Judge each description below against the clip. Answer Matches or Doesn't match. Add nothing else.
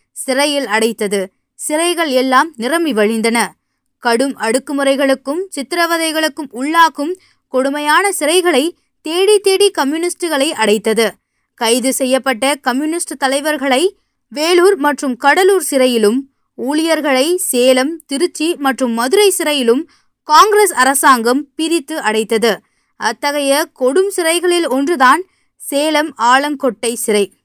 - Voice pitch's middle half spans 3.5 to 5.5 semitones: Matches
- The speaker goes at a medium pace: Matches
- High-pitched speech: Matches